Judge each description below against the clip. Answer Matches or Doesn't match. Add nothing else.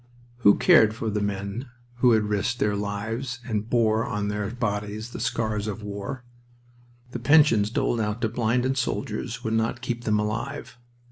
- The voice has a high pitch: Doesn't match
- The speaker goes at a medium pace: Matches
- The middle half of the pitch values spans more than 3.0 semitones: Doesn't match